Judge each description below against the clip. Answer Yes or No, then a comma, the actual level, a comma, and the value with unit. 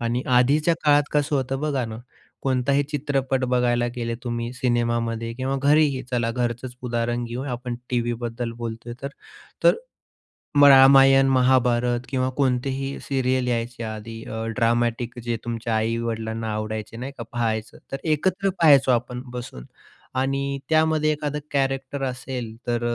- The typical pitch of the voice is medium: No, low, 125 Hz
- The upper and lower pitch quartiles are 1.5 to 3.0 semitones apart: Yes, narrow, 2.5 semitones